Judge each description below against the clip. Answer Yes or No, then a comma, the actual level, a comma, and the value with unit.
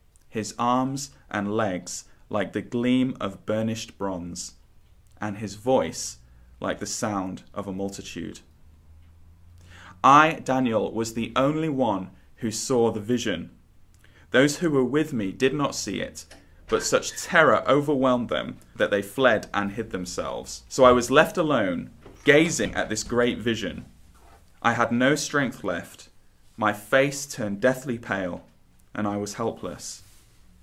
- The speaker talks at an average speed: Yes, average, 145 wpm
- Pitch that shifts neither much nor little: No, wide, 5.9 semitones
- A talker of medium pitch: No, low, 110 Hz